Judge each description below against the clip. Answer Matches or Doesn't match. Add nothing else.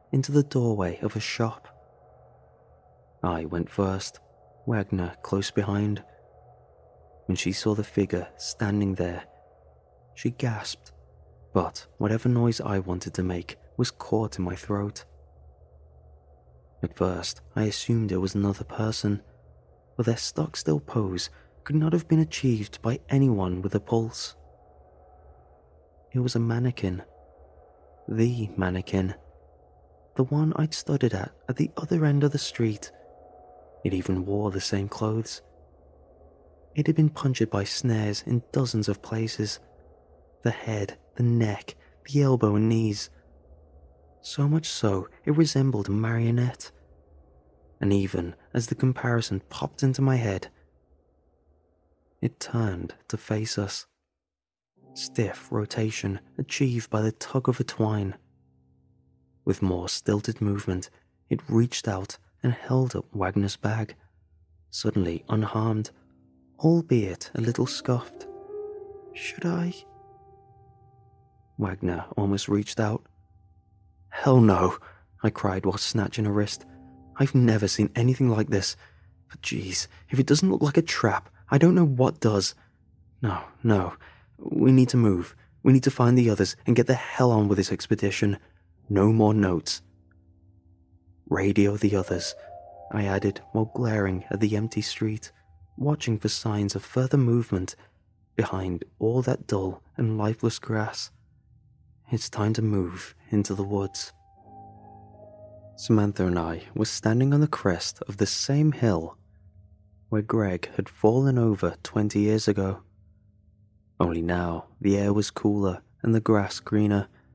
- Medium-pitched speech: Doesn't match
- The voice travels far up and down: Doesn't match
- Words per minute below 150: Matches